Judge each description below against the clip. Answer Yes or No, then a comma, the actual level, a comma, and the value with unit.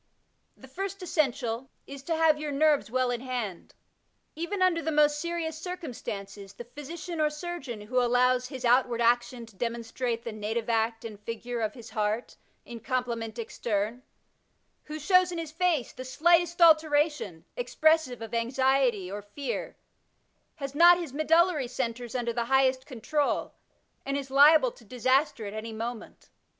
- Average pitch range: Yes, average, 5.0 semitones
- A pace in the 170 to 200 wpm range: No, average, 160 wpm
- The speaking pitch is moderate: No, very high, 255 Hz